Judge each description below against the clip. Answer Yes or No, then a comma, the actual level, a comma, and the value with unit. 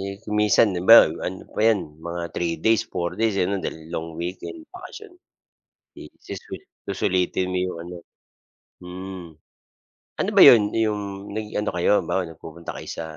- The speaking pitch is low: Yes, very low, 95 Hz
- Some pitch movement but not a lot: Yes, average, 3.4 semitones